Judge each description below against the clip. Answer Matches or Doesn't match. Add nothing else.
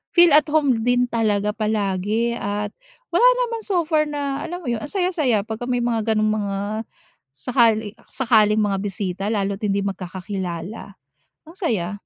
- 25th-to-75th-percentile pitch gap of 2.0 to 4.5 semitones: Doesn't match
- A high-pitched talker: Matches